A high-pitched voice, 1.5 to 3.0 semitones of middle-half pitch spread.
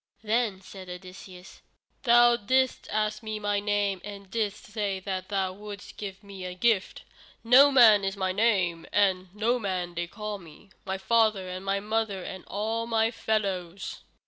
Yes: high, 200 Hz; average, 2.7 semitones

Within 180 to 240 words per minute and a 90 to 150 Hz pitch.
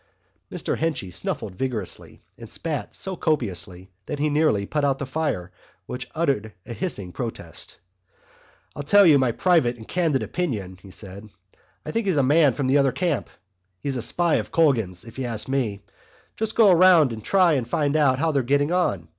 Yes: average, 190 wpm; low, 135 Hz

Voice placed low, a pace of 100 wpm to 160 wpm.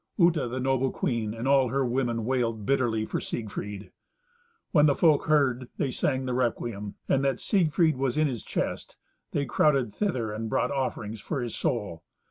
No: low, 130 Hz; average, 175 wpm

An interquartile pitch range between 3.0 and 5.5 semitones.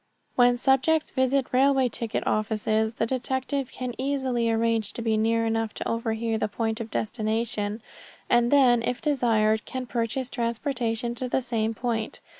No: narrow, 2.5 semitones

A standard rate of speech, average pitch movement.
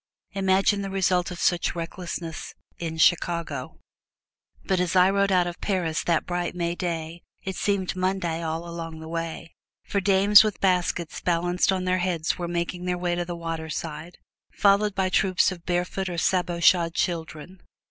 No: average, 170 wpm; narrow, 1.9 semitones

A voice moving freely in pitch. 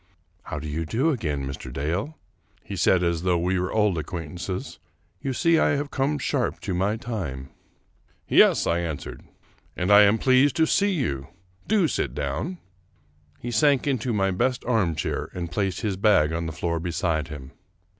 Yes: wide, 7.2 semitones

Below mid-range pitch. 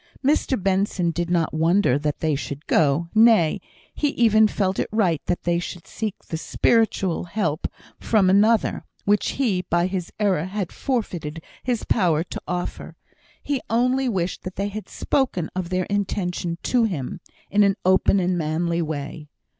No: medium, 185 Hz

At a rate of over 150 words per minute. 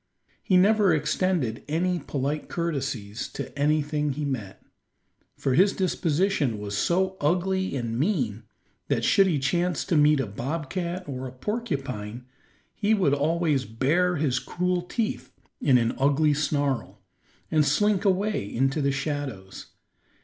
No: slow, 135 wpm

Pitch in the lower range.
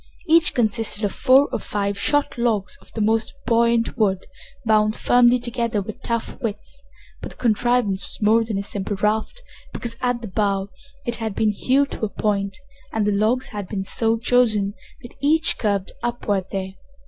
No: high, 220 Hz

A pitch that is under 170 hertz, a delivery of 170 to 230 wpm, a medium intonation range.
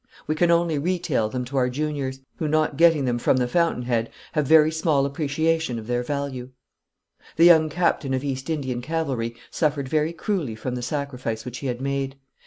Yes: medium, 140 Hz; average, 195 wpm; average, 3.9 semitones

